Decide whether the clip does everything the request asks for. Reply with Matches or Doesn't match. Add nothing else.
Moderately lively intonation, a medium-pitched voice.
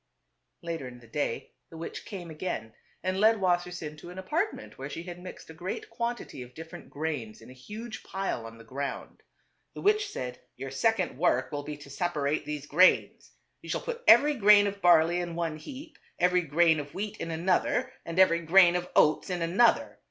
Matches